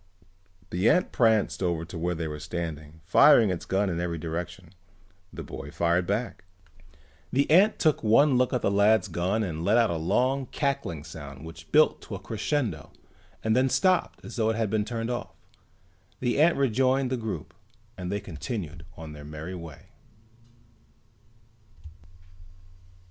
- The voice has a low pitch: Yes, low, 100 Hz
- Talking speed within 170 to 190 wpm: No, average, 160 wpm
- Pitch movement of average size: No, wide, 6.8 semitones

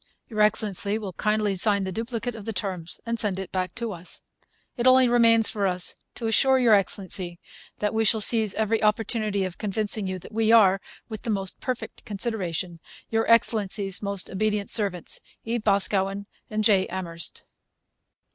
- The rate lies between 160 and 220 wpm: Yes, average, 165 wpm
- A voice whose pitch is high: Yes, high, 210 Hz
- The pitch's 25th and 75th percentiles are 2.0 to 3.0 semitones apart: Yes, average, 2.7 semitones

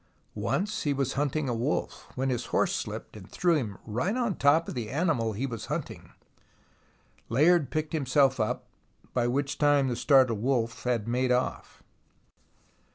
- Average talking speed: Yes, average, 160 wpm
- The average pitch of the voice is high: No, low, 135 Hz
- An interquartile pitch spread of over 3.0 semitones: Yes, average, 3.7 semitones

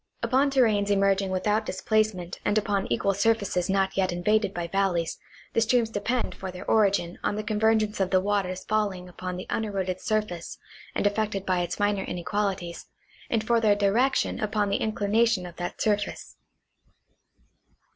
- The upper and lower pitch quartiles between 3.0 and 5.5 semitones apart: No, narrow, 2.6 semitones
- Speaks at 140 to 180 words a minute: Yes, average, 160 wpm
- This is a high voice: Yes, high, 205 Hz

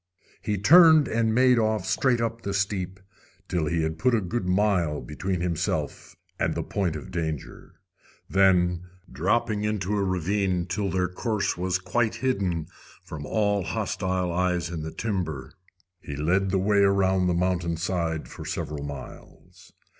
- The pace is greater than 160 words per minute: No, average, 155 wpm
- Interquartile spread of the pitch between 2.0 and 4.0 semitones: Yes, average, 3.4 semitones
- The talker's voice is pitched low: Yes, very low, 95 Hz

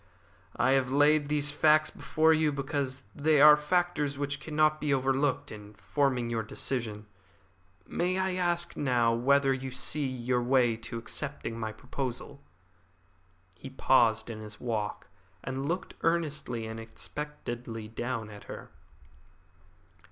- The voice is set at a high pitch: No, low, 135 Hz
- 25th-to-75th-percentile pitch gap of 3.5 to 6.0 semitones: Yes, average, 4.3 semitones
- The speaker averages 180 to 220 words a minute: No, slow, 135 wpm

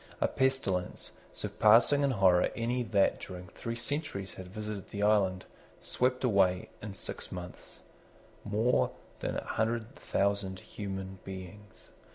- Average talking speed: No, slow, 130 wpm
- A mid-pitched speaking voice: No, low, 105 Hz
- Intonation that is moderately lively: Yes, average, 3.6 semitones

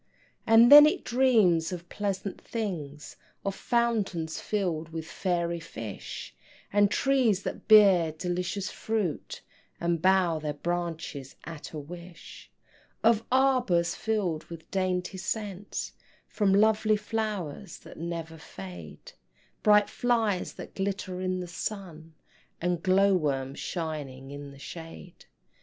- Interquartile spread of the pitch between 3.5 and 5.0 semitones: Yes, average, 4.3 semitones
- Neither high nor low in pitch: Yes, medium, 180 Hz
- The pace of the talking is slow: Yes, slow, 120 wpm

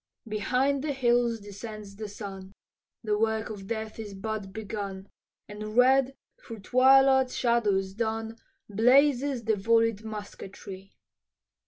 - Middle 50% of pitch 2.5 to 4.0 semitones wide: Yes, average, 3.1 semitones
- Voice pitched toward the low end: No, high, 220 Hz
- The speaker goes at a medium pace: No, slow, 120 wpm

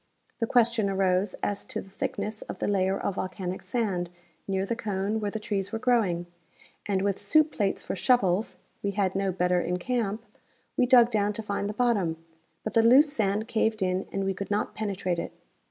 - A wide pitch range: No, average, 2.8 semitones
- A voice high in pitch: Yes, high, 200 Hz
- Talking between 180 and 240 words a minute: Yes, average, 200 wpm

